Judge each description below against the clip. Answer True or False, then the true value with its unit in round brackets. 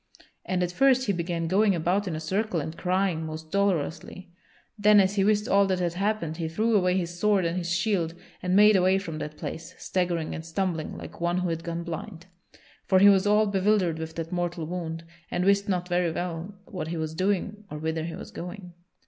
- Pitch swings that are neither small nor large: True (3.1 semitones)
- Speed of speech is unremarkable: False (215 wpm)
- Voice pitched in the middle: True (180 Hz)